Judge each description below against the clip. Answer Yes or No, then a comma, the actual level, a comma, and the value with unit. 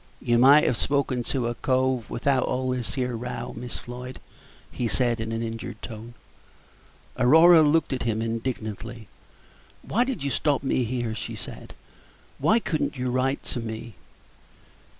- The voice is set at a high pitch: No, low, 125 Hz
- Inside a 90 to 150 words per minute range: No, average, 160 wpm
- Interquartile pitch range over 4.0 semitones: No, narrow, 2.6 semitones